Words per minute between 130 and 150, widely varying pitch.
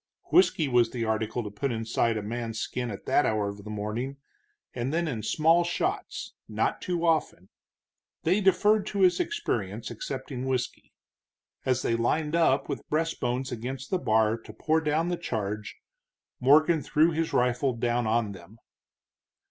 No: average, 160 wpm; wide, 6.2 semitones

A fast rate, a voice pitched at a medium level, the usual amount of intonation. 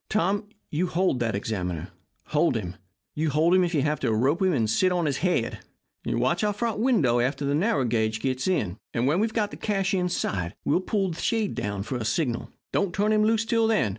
No: fast, 220 wpm; medium, 160 Hz; wide, 8.7 semitones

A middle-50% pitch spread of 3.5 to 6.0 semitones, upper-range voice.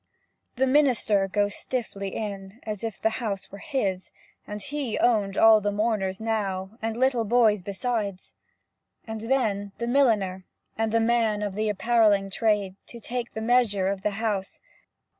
No: average, 2.9 semitones; high, 215 Hz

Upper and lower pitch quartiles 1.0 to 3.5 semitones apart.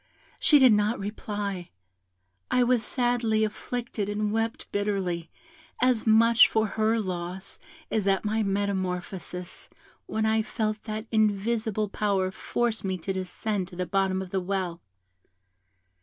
Yes: narrow, 2.6 semitones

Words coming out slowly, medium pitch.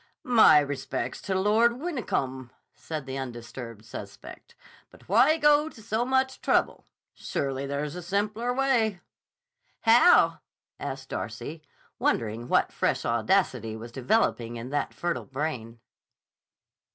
Yes: slow, 120 wpm; medium, 150 Hz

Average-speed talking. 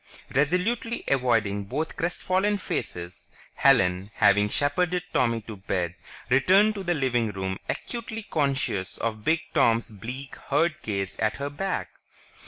No: slow, 130 wpm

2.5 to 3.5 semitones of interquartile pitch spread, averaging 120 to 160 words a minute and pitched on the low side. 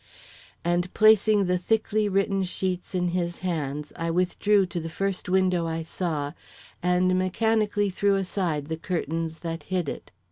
No: average, 2.9 semitones; average, 150 wpm; medium, 180 Hz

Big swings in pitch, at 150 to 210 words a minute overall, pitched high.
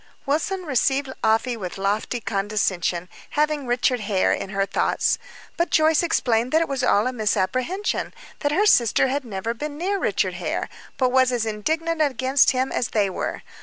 Yes: wide, 5.8 semitones; average, 170 wpm; very high, 255 Hz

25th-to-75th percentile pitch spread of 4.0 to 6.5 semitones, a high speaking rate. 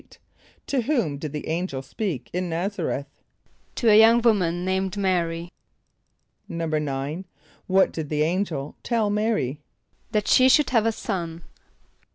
No: average, 5.2 semitones; average, 145 wpm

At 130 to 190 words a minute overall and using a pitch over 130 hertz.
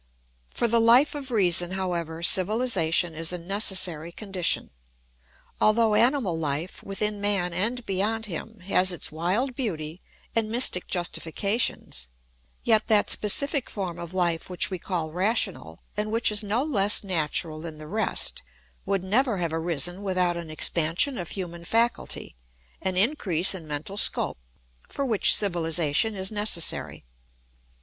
Yes: average, 140 wpm; high, 190 Hz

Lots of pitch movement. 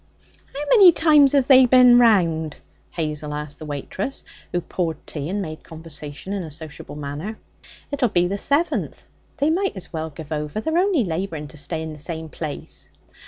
Yes: wide, 8.5 semitones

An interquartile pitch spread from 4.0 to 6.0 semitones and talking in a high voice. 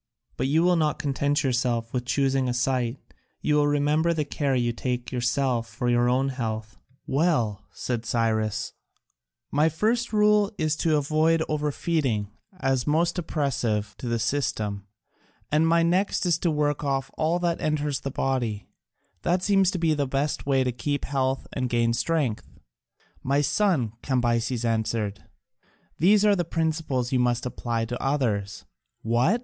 No: average, 4.7 semitones; low, 135 Hz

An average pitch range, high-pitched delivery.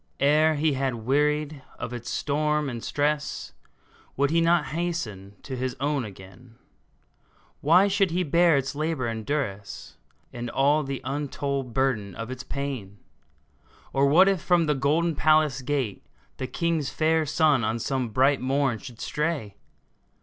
No: average, 3.6 semitones; medium, 140 Hz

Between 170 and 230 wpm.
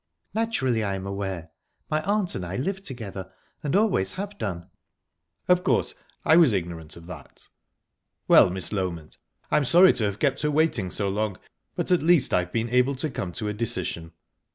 Yes: average, 180 wpm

